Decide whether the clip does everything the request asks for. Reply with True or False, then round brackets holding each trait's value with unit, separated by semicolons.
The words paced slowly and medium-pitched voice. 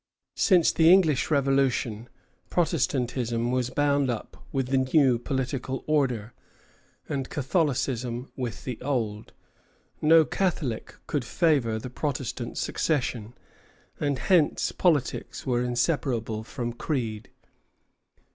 False (105 wpm; 130 Hz)